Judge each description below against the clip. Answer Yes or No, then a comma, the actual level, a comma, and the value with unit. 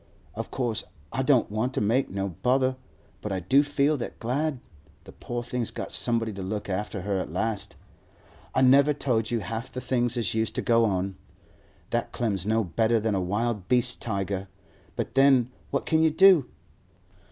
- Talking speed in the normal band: Yes, average, 185 wpm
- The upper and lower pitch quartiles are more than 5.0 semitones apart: No, average, 4.0 semitones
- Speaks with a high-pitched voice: No, low, 115 Hz